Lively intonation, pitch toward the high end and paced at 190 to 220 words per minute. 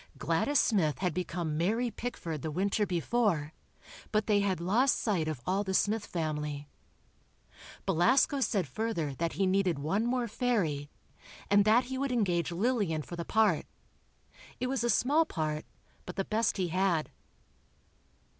No: wide, 5.7 semitones; high, 195 Hz; average, 155 wpm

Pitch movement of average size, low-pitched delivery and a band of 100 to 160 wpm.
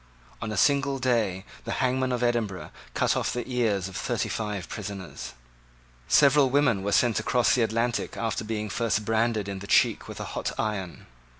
No: average, 3.4 semitones; low, 115 Hz; average, 180 wpm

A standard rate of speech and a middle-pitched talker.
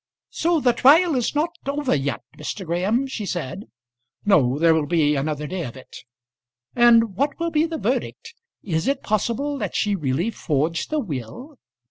No: average, 170 wpm; high, 210 Hz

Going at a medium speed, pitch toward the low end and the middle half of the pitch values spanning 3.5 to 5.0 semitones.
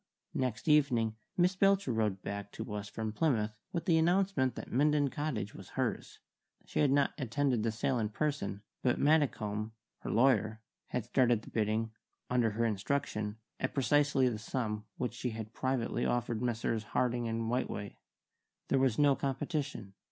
Yes: average, 160 wpm; low, 120 Hz; average, 4.5 semitones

